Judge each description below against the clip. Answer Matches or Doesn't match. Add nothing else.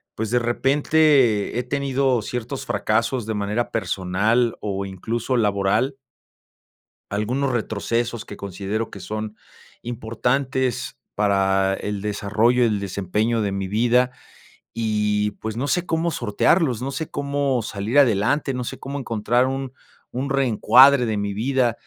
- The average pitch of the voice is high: Doesn't match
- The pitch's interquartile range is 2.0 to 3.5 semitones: Doesn't match